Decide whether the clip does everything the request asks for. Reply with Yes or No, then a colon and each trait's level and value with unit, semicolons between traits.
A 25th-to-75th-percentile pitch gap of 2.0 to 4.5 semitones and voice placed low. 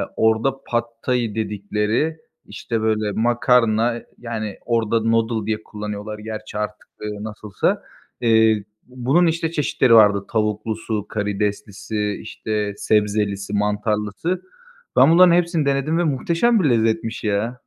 Yes: narrow, 2.6 semitones; low, 110 Hz